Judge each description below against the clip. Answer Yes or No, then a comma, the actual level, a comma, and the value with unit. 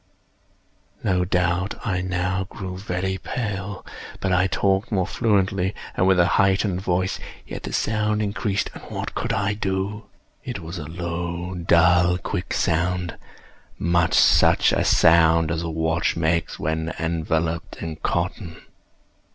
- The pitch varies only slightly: Yes, narrow, 2.3 semitones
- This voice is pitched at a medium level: No, very low, 90 Hz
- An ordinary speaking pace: No, slow, 130 wpm